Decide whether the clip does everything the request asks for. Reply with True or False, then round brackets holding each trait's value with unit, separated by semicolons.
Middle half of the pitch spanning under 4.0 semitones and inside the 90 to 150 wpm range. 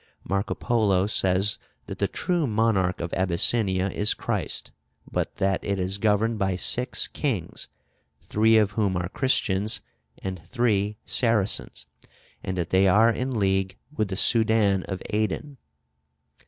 True (2.9 semitones; 140 wpm)